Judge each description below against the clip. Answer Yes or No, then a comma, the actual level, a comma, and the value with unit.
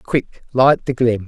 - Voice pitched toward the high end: No, low, 125 Hz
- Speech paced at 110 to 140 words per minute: No, average, 190 wpm